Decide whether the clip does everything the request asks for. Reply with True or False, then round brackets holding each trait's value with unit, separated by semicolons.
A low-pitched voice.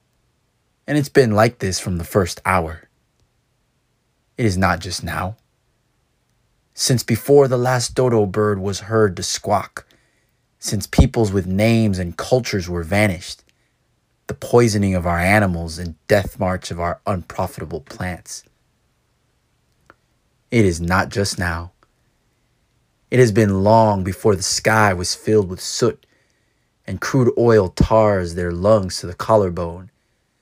True (100 Hz)